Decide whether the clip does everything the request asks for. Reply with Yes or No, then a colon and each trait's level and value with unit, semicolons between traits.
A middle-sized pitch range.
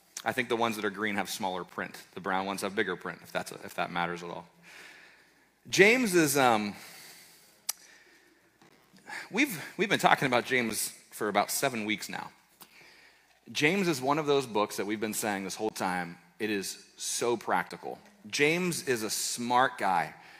No: wide, 5.7 semitones